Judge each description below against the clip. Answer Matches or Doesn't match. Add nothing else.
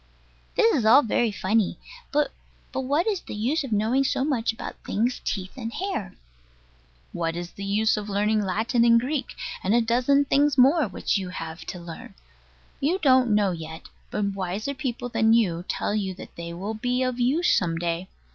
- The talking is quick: Doesn't match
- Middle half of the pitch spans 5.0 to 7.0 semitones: Matches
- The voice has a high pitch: Matches